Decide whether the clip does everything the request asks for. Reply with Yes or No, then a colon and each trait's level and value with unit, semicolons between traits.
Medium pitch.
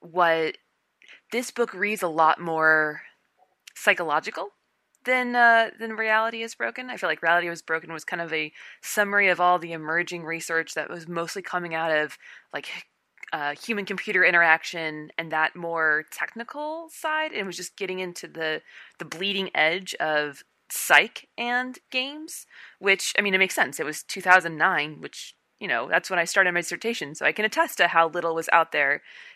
Yes: medium, 175 Hz